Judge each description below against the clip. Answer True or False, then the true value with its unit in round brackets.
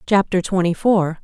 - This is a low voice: False (185 Hz)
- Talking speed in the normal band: True (145 wpm)